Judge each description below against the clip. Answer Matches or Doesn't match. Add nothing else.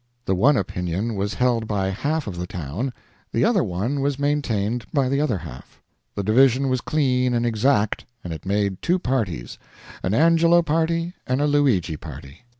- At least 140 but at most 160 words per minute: Doesn't match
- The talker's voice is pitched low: Matches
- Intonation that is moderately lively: Doesn't match